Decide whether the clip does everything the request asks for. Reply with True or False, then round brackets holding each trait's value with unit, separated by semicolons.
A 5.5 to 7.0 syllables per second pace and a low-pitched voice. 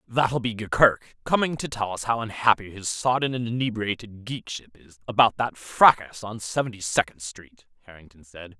False (5.1 syllables/s; 110 Hz)